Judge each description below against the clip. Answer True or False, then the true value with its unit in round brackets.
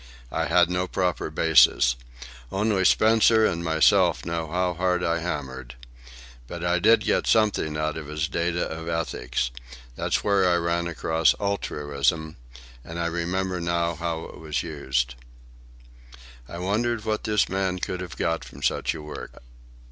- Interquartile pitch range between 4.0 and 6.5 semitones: False (2.5 semitones)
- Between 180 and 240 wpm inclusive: False (155 wpm)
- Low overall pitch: True (85 Hz)